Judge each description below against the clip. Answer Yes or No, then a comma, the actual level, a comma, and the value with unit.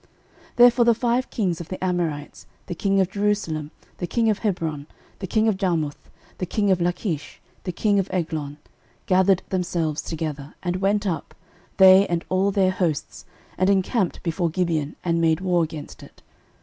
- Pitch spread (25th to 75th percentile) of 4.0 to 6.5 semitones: No, average, 3.4 semitones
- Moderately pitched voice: Yes, medium, 180 Hz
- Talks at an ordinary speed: Yes, average, 175 wpm